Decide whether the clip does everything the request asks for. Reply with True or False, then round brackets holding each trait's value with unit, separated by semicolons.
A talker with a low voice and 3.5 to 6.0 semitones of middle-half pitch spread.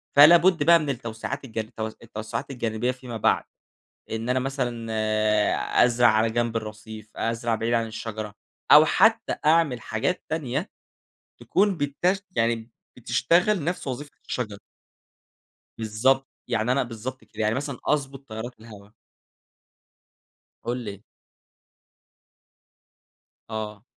True (120 Hz; 4.0 semitones)